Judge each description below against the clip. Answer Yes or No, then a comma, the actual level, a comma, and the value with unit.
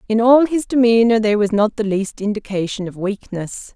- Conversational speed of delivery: Yes, average, 190 wpm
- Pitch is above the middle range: Yes, high, 215 Hz